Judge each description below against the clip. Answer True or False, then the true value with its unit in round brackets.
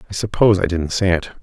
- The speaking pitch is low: True (95 Hz)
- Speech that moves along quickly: True (255 wpm)